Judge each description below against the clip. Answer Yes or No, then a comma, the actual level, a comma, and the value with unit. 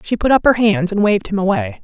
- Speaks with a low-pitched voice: No, high, 210 Hz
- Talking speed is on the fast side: Yes, fast, 295 wpm